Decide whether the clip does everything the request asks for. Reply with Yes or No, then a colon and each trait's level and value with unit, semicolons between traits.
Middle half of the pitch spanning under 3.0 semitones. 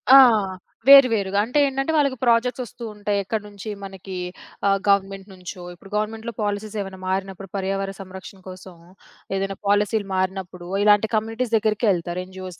Yes: narrow, 2.6 semitones